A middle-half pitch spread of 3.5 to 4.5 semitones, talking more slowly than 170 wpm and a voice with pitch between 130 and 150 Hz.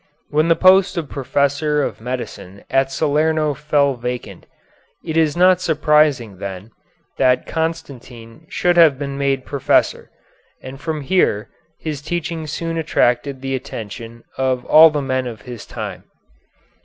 Yes: average, 4.0 semitones; average, 140 wpm; medium, 140 Hz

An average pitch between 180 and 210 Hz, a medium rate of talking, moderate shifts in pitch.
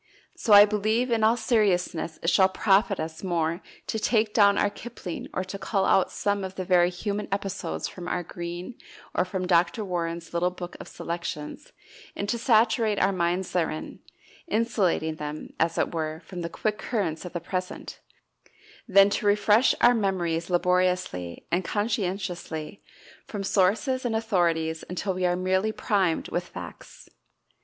Yes: medium, 185 Hz; average, 160 wpm; average, 3.2 semitones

